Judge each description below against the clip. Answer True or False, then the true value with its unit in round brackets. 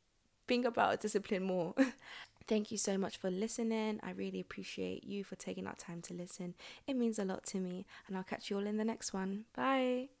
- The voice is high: True (200 Hz)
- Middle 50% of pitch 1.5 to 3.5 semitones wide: True (3.2 semitones)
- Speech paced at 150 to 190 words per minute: False (205 wpm)